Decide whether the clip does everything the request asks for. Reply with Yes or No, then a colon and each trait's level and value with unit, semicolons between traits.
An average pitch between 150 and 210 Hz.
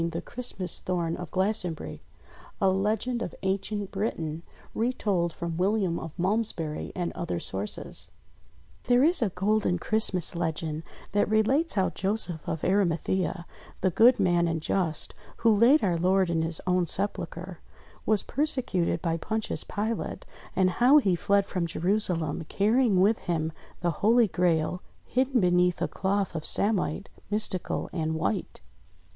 Yes: medium, 185 Hz